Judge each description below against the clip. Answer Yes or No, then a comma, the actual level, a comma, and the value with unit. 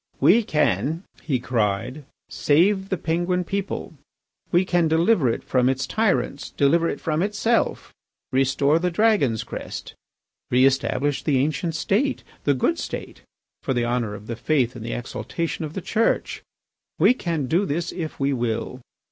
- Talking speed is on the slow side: No, average, 155 wpm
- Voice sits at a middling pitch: Yes, medium, 150 Hz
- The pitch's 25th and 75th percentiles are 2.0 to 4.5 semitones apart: No, wide, 5.5 semitones